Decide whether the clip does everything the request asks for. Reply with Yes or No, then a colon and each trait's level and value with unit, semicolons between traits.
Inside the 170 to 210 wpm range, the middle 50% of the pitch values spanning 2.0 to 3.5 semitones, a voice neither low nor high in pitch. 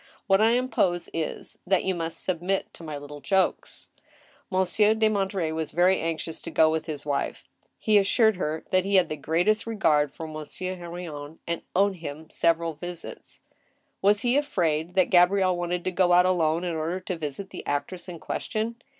Yes: average, 185 wpm; average, 3.2 semitones; medium, 175 Hz